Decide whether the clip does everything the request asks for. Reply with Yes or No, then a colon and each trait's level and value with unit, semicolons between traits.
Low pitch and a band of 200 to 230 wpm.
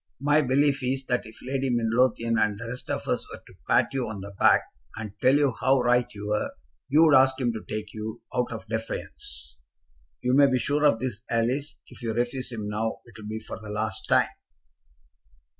Yes: low, 120 Hz; fast, 205 wpm